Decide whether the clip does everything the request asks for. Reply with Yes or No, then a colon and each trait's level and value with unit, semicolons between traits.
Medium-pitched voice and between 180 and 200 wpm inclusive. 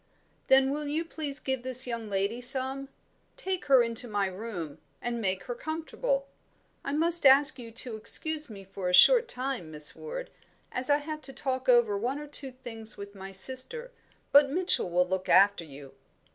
No: very high, 255 Hz; average, 185 wpm